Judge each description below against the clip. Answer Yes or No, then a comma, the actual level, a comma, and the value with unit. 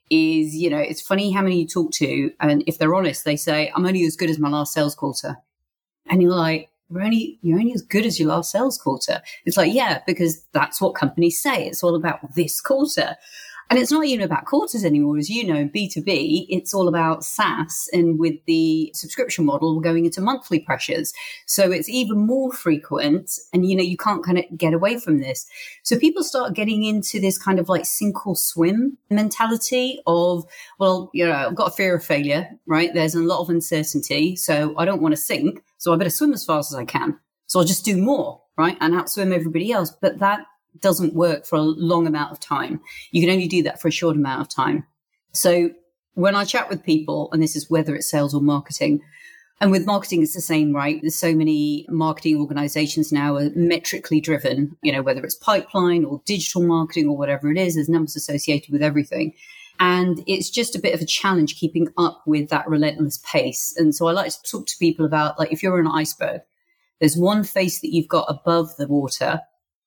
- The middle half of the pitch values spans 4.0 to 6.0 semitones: No, average, 3.6 semitones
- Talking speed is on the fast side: Yes, fast, 215 wpm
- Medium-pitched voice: Yes, medium, 170 Hz